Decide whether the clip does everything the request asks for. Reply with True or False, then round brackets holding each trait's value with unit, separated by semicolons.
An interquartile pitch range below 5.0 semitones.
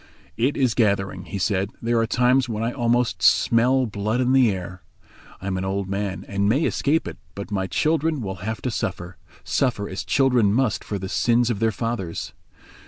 True (4.0 semitones)